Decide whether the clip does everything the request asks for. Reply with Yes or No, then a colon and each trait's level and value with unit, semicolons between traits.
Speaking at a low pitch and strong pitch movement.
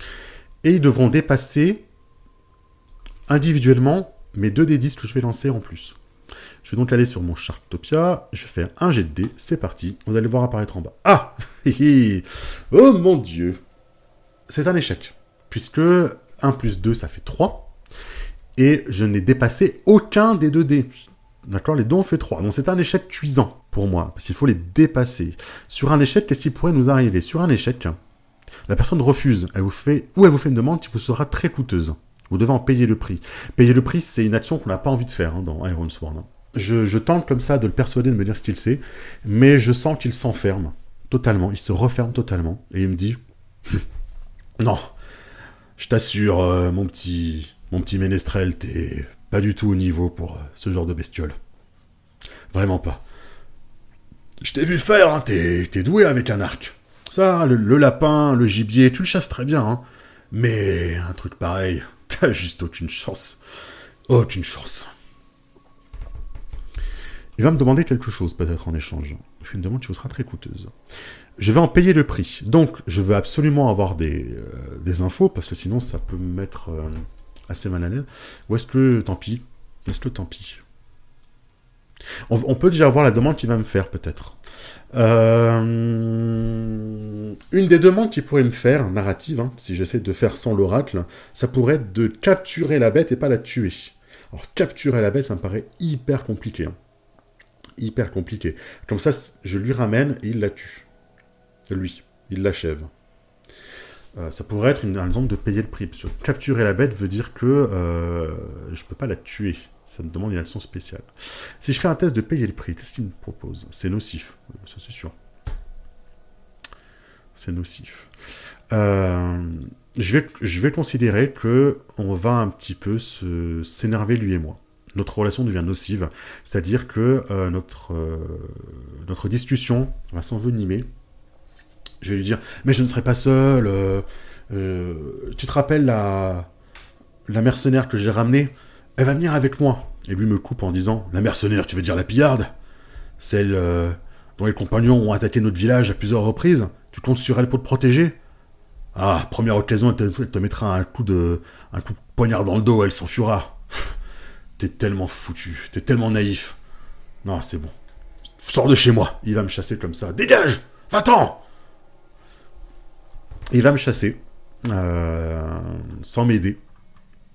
Yes: low, 110 Hz; wide, 6.0 semitones